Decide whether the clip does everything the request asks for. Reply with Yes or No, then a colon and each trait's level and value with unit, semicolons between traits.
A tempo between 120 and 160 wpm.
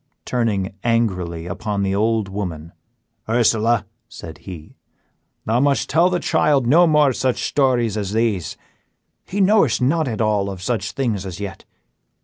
Yes: average, 145 wpm